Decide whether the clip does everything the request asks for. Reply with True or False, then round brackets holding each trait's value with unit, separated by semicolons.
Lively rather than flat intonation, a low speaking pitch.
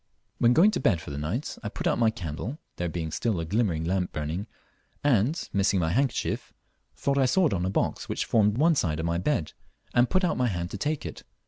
True (7.2 semitones; 105 Hz)